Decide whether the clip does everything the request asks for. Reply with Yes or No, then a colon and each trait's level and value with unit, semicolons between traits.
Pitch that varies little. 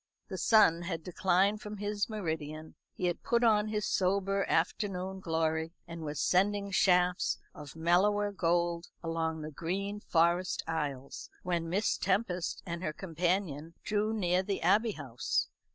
No: average, 3.5 semitones